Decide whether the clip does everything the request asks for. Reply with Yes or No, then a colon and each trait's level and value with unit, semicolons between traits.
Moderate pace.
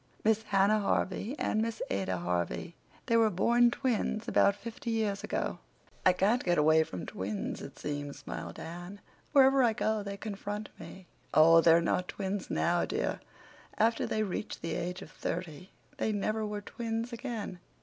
Yes: average, 165 wpm